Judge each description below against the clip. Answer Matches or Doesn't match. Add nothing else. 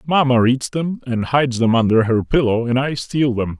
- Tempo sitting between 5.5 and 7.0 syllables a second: Doesn't match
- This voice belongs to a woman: Doesn't match